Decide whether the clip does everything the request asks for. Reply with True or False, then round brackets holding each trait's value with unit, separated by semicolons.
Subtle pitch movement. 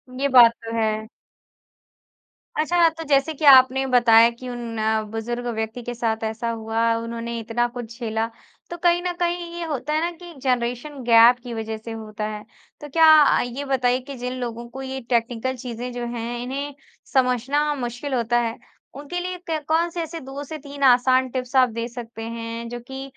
False (3.5 semitones)